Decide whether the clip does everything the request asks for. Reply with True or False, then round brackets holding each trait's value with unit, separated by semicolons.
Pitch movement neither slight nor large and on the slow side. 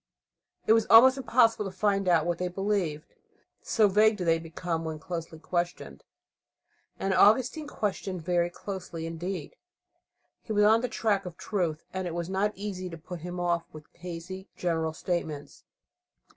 False (3.7 semitones; 160 wpm)